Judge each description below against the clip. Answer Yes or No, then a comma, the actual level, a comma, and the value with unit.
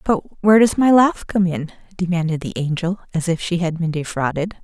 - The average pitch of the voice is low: No, medium, 180 Hz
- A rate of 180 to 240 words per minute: Yes, fast, 205 wpm